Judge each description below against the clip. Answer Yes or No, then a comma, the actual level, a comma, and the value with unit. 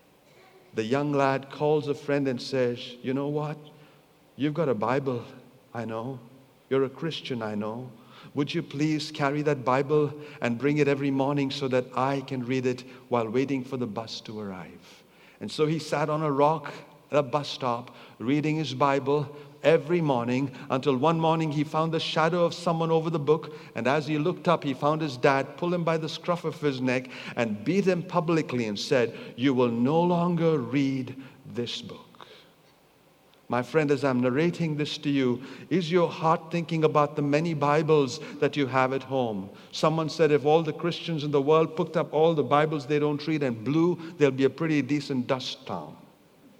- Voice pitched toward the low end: No, medium, 145 Hz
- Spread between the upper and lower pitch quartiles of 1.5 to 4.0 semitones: Yes, average, 3.2 semitones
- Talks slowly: No, average, 195 wpm